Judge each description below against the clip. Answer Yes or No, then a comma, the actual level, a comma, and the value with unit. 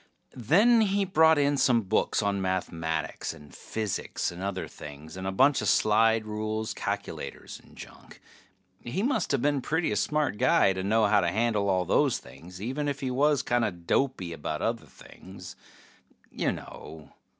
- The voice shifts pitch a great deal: Yes, wide, 6.9 semitones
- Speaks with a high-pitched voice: No, low, 110 Hz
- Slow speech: No, average, 165 wpm